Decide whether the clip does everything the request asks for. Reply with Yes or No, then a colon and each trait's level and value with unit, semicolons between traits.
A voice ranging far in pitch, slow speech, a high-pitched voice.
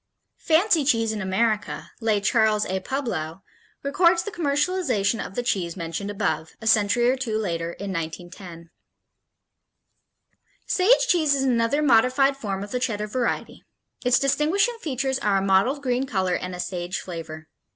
No: wide, 6.3 semitones; average, 150 wpm; high, 225 Hz